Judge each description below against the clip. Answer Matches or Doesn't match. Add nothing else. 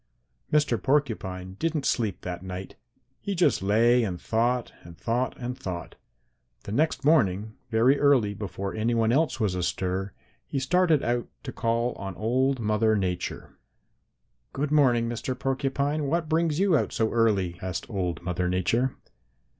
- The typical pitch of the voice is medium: Doesn't match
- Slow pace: Doesn't match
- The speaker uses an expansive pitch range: Matches